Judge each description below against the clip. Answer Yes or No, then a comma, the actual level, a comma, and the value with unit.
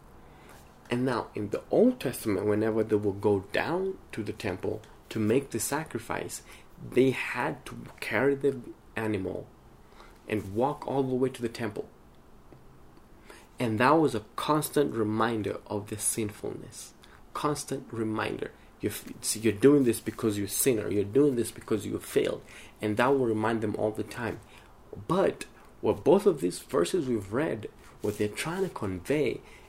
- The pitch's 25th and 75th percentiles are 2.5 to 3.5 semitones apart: No, average, 3.9 semitones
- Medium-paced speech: Yes, average, 155 wpm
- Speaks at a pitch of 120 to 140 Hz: No, low, 110 Hz